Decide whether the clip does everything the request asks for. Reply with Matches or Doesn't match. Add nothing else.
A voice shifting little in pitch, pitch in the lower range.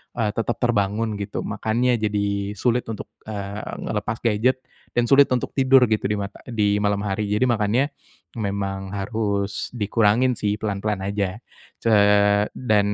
Matches